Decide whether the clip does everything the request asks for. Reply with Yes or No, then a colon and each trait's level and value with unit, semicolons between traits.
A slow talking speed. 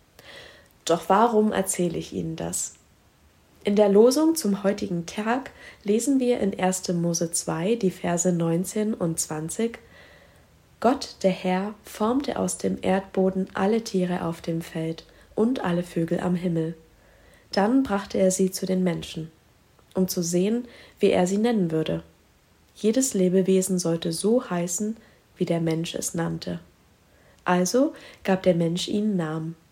No: average, 145 wpm